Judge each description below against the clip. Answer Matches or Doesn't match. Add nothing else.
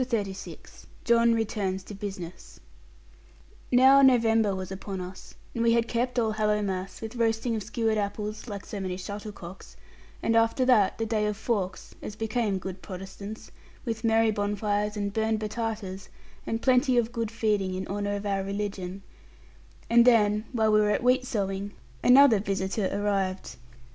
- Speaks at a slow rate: Doesn't match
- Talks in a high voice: Matches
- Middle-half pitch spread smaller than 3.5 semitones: Matches